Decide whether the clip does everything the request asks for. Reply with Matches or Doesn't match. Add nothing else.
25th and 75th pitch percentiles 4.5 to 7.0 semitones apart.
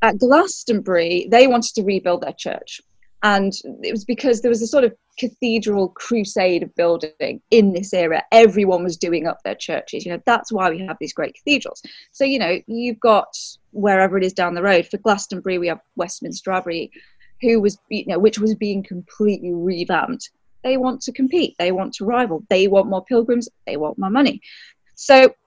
Matches